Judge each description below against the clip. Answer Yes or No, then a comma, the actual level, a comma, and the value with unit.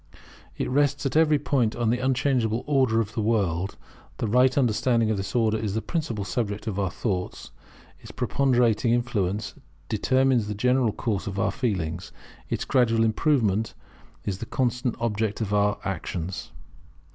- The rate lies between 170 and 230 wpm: No, average, 155 wpm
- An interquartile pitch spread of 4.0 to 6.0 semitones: No, average, 3.6 semitones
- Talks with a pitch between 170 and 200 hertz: No, low, 115 Hz